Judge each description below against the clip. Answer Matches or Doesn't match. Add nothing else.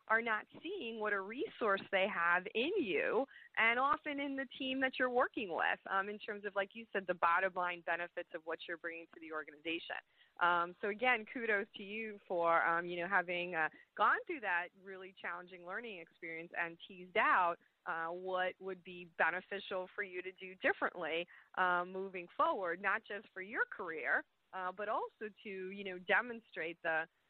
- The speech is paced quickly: Doesn't match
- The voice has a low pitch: Doesn't match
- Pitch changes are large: Doesn't match